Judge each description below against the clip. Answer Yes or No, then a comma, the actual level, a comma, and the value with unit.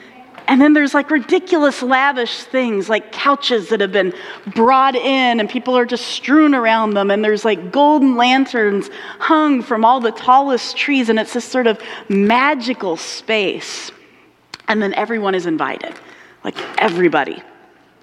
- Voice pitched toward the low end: No, high, 245 Hz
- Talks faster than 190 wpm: No, average, 155 wpm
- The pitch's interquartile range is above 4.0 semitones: No, average, 3.6 semitones